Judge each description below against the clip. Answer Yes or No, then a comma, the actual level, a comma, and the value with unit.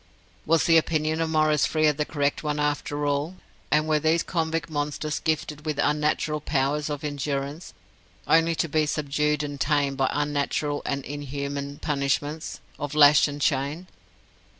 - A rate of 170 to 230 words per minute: No, average, 150 wpm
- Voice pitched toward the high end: No, medium, 150 Hz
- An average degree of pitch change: No, narrow, 1.4 semitones